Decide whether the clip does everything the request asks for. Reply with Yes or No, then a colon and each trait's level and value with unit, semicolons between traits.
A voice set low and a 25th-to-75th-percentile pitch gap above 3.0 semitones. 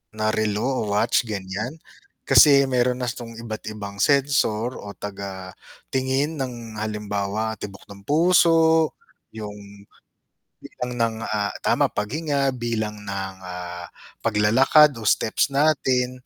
Yes: low, 110 Hz; average, 4.4 semitones